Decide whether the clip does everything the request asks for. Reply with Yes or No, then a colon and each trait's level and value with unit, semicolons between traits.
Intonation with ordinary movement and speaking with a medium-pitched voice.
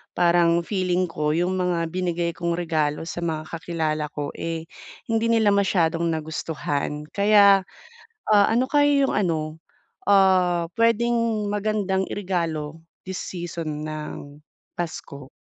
Yes: average, 4.0 semitones; medium, 175 Hz